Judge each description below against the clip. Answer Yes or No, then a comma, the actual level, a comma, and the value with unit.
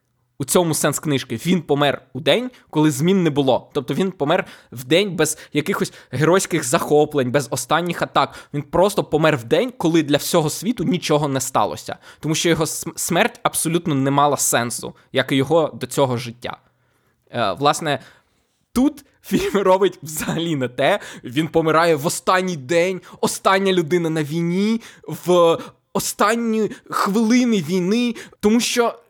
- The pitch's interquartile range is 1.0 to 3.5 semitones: No, average, 4.6 semitones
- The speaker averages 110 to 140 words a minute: No, fast, 155 wpm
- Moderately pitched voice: Yes, medium, 165 Hz